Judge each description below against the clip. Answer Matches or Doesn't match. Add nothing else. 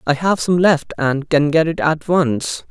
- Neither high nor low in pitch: Matches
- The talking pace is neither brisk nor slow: Doesn't match